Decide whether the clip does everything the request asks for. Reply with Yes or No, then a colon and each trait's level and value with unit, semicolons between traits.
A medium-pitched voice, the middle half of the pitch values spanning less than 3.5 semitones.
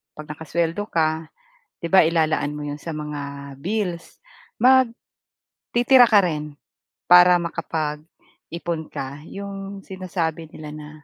Yes: medium, 165 Hz; average, 3.1 semitones